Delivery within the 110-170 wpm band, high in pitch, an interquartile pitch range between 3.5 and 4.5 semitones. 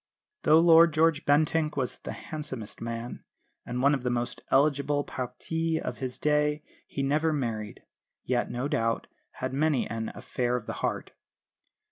No: average, 160 wpm; medium, 140 Hz; average, 3.8 semitones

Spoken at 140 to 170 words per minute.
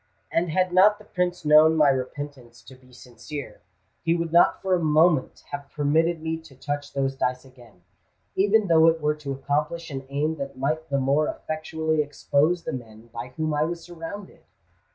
No: average, 180 wpm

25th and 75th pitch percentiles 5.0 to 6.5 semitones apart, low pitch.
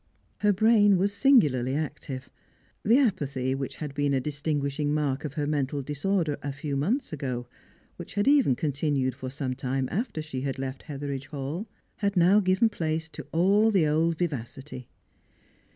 No: wide, 5.5 semitones; medium, 150 Hz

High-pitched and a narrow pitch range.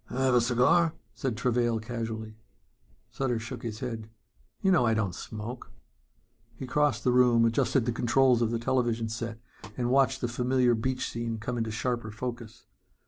No: low, 120 Hz; narrow, 1.9 semitones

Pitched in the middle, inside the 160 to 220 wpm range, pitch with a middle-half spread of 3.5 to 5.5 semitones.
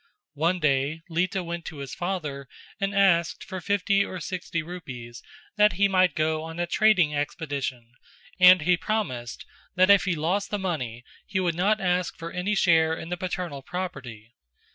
Yes: medium, 175 Hz; average, 170 wpm; average, 3.8 semitones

